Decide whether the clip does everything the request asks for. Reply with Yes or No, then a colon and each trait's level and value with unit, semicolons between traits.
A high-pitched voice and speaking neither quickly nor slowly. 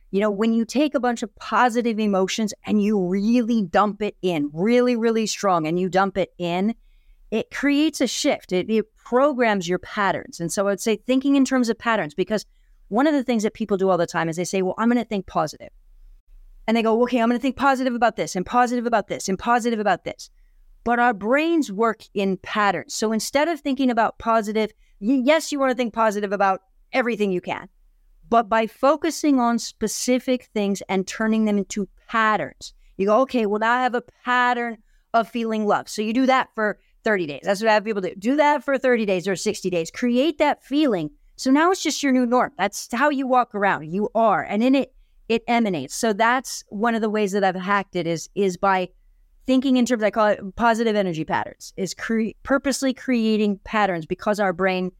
No: high, 220 Hz; fast, 220 wpm